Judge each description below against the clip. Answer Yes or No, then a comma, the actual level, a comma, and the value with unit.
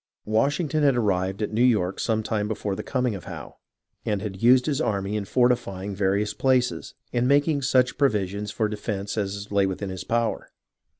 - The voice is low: Yes, low, 105 Hz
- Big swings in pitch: No, average, 4.1 semitones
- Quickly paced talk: No, average, 180 wpm